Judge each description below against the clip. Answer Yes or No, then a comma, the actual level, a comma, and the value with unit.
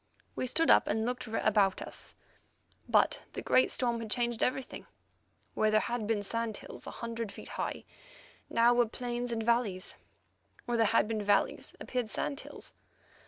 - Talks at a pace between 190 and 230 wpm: No, average, 165 wpm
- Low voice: No, high, 230 Hz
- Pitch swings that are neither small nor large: No, narrow, 2.0 semitones